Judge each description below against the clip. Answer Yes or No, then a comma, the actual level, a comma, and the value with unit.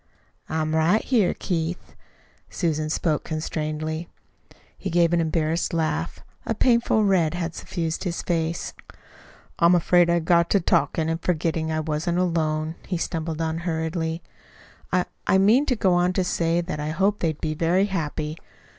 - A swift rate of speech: No, average, 160 wpm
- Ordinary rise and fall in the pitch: No, narrow, 2.1 semitones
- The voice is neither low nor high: Yes, medium, 165 Hz